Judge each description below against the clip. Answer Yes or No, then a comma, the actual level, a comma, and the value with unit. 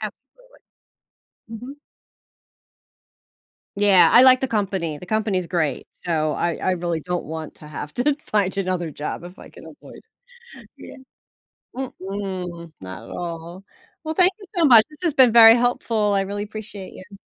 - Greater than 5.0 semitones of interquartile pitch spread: Yes, wide, 5.4 semitones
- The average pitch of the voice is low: No, high, 195 Hz